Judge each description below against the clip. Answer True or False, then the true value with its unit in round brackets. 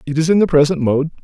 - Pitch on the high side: False (155 Hz)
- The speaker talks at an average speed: False (290 wpm)